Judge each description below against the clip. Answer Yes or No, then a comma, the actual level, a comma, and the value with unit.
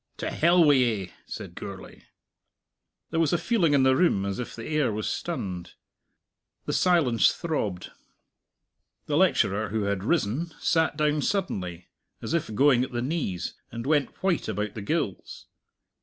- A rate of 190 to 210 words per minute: No, average, 155 wpm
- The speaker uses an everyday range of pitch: No, wide, 7.7 semitones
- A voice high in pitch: No, low, 130 Hz